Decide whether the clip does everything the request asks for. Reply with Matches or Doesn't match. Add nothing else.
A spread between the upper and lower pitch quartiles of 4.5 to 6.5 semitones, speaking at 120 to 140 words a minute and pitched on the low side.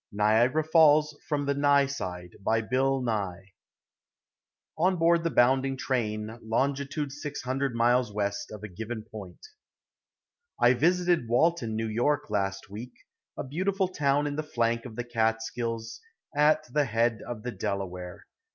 Matches